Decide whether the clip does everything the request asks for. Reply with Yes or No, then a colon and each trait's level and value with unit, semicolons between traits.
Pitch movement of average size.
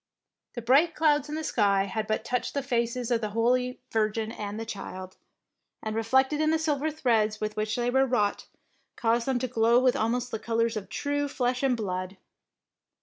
Yes: average, 3.4 semitones